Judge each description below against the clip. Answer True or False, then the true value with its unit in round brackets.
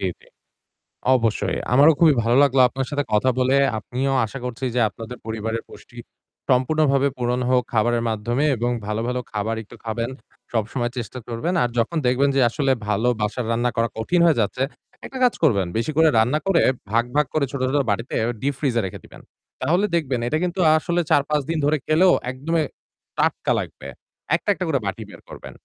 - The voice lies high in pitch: False (125 Hz)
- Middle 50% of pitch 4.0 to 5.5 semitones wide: True (4.3 semitones)